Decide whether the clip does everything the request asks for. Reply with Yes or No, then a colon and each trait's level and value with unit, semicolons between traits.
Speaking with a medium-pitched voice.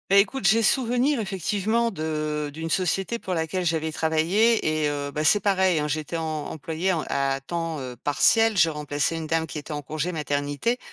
Yes: medium, 160 Hz